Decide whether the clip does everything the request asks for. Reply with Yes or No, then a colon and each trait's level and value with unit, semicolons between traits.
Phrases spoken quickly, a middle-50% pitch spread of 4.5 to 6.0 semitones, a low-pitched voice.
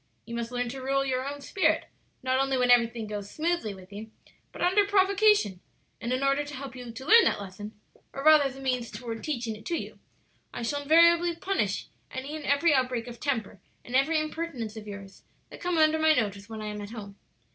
No: fast, 220 wpm; wide, 5.5 semitones; very high, 260 Hz